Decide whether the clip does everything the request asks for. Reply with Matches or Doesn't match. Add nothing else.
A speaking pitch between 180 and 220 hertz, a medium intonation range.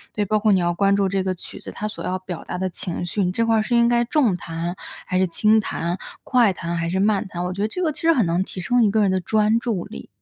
Matches